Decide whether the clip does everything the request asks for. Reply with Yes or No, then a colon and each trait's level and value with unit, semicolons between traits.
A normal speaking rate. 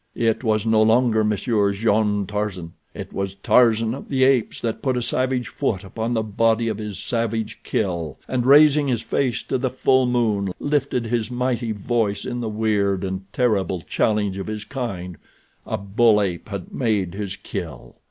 Yes: average, 170 wpm